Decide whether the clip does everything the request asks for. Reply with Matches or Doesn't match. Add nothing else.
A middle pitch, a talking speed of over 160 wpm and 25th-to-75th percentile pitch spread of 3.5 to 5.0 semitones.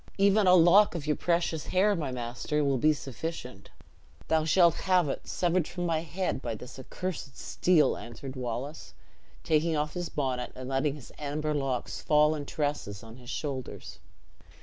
Matches